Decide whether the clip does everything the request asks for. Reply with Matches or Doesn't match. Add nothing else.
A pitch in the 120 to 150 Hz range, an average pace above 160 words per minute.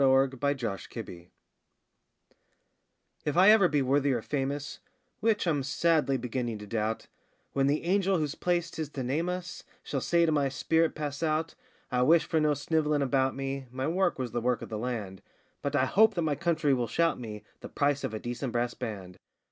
Matches